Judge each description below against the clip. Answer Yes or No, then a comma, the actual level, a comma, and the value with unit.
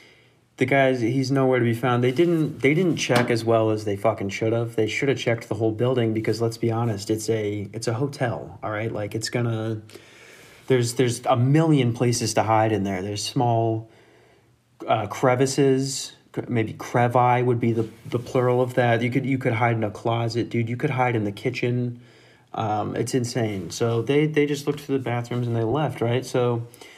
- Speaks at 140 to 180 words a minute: No, fast, 205 wpm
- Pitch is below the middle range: Yes, low, 120 Hz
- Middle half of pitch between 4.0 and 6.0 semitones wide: No, narrow, 2.6 semitones